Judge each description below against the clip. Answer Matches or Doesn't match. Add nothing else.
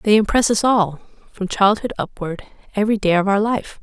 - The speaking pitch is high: Matches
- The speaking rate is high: Doesn't match